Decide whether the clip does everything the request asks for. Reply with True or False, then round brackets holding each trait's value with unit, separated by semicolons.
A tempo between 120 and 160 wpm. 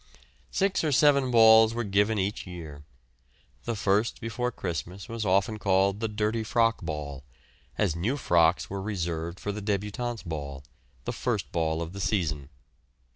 True (155 wpm)